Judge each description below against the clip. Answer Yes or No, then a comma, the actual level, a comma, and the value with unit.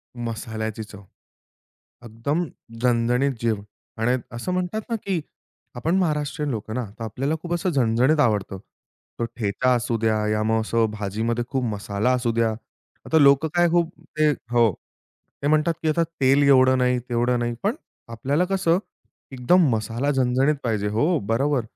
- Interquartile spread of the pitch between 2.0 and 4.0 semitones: No, average, 5.1 semitones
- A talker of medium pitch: No, low, 125 Hz